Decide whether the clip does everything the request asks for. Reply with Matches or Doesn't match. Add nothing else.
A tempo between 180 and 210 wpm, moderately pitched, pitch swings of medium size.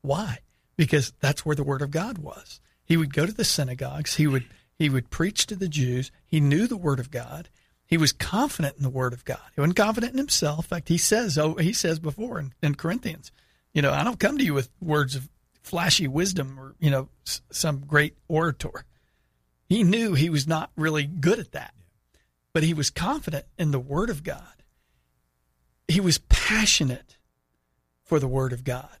Matches